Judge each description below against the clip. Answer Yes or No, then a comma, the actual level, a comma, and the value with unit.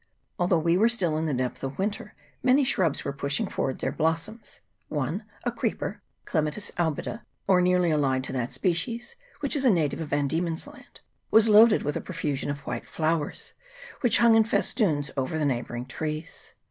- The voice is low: No, medium, 165 Hz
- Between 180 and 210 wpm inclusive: Yes, average, 185 wpm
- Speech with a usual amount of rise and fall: No, wide, 6.5 semitones